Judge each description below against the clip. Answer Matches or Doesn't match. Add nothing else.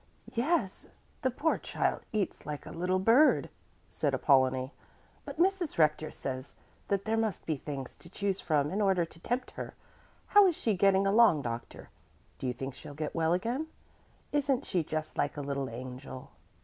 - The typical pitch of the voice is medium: Matches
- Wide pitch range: Matches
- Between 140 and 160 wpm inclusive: Doesn't match